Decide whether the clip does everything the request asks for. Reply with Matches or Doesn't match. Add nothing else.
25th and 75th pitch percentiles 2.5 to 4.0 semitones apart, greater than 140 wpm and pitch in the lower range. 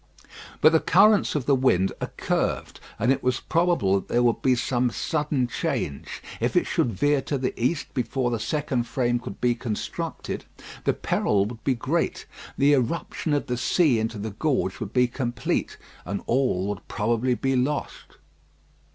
Matches